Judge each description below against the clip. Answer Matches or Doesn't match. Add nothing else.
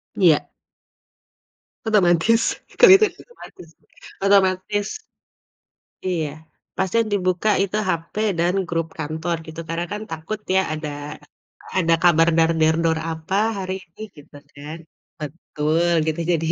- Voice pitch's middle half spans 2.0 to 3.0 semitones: Doesn't match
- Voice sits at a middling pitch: Matches